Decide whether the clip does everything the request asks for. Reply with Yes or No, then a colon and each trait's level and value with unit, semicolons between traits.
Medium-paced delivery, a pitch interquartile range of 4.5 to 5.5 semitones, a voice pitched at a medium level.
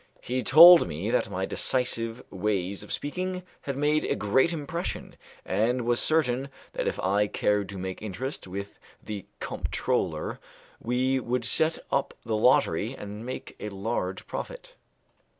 No: average, 150 wpm; average, 5.0 semitones; low, 115 Hz